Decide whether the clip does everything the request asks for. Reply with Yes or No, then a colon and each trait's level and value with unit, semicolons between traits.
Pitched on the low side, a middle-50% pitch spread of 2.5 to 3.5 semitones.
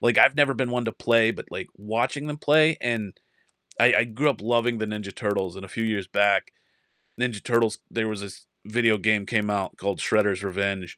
Yes: low, 110 Hz; average, 2.9 semitones